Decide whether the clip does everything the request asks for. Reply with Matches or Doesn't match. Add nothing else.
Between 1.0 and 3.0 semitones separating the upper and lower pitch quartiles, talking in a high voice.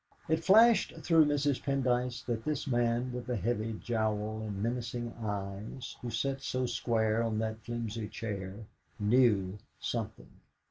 Doesn't match